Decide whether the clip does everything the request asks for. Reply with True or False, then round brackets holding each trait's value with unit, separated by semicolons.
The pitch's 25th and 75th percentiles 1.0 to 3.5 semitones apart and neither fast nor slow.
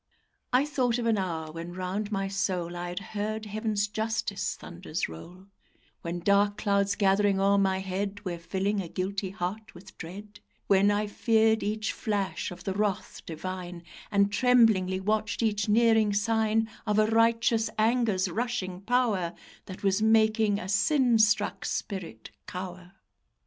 True (2.7 semitones; 150 wpm)